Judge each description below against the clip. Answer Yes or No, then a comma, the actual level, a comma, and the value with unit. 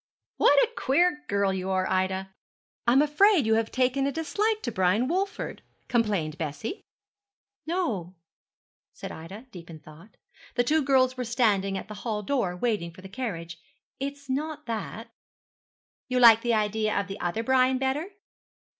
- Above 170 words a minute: No, average, 165 wpm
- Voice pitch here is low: No, high, 230 Hz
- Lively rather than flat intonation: Yes, wide, 6.1 semitones